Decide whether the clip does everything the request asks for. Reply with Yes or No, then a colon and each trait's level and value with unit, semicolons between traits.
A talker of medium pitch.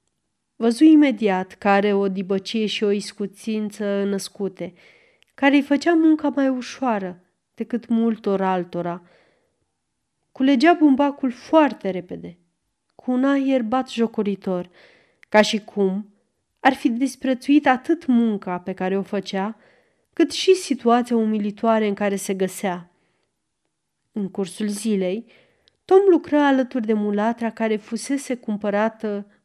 No: high, 220 Hz